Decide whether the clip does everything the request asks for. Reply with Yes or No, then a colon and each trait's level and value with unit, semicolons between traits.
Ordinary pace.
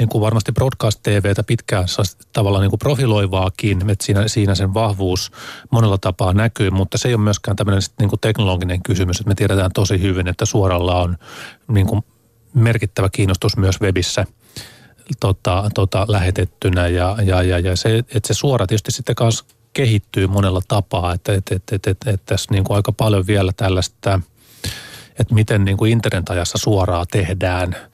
No: fast, 165 wpm